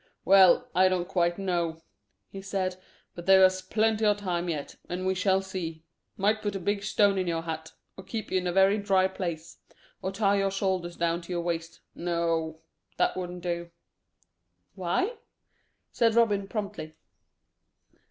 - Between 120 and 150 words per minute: No, average, 160 wpm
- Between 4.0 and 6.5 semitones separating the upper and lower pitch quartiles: No, narrow, 2.4 semitones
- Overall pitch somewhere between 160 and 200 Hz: Yes, medium, 185 Hz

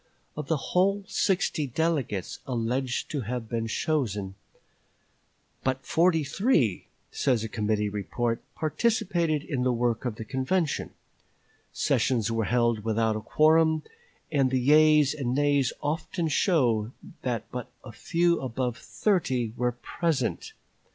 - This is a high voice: No, low, 130 Hz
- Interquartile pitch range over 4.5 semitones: Yes, average, 5.3 semitones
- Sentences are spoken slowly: Yes, slow, 125 wpm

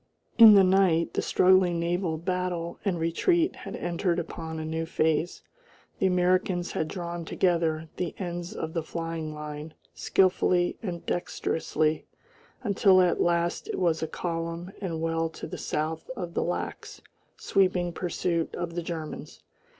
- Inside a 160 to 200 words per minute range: No, average, 150 wpm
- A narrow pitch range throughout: Yes, narrow, 1.9 semitones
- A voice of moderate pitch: Yes, medium, 170 Hz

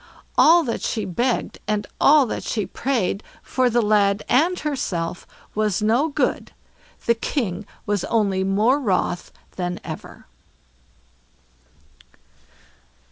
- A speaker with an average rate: No, slow, 115 wpm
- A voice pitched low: No, high, 215 Hz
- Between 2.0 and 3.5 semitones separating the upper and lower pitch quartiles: No, average, 4.6 semitones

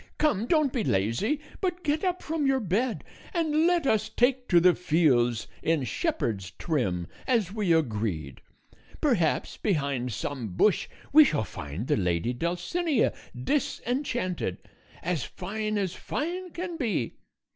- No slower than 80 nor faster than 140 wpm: Yes, slow, 135 wpm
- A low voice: No, high, 195 Hz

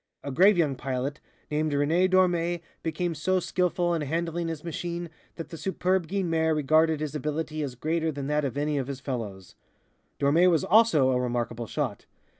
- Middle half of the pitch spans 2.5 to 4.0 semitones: Yes, average, 3.5 semitones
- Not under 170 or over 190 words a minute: Yes, average, 175 wpm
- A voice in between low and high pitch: Yes, medium, 155 Hz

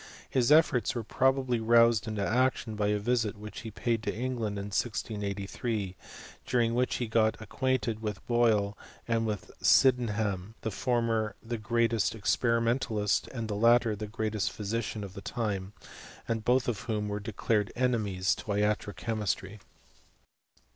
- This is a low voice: Yes, low, 110 Hz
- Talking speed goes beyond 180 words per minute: No, average, 155 wpm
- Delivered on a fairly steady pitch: Yes, narrow, 2.2 semitones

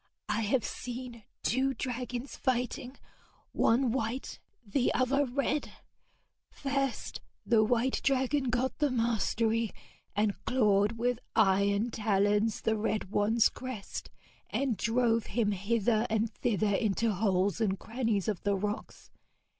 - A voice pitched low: No, high, 230 Hz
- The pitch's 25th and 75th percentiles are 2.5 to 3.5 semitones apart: Yes, average, 3.2 semitones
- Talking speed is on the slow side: Yes, slow, 120 wpm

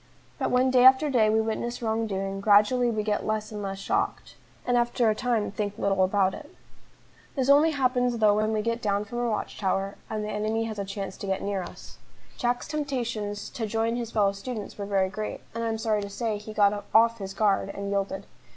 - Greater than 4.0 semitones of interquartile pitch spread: No, average, 2.9 semitones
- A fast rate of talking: Yes, fast, 225 wpm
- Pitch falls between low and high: No, high, 215 Hz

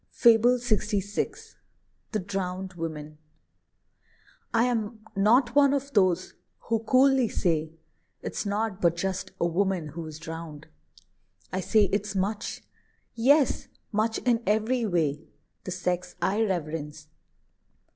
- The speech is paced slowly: Yes, slow, 120 wpm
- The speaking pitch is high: Yes, high, 200 Hz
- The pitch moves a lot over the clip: No, average, 4.9 semitones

